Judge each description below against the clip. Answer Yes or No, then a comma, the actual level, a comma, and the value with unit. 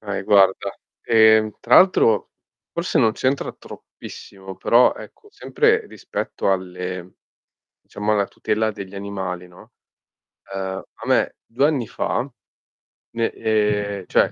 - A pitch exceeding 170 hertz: No, low, 105 Hz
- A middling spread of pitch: Yes, average, 3.1 semitones